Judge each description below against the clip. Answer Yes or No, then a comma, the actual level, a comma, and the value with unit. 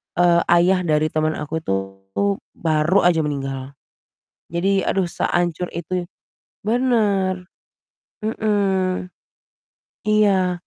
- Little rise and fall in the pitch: No, average, 3.7 semitones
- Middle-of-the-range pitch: Yes, medium, 180 Hz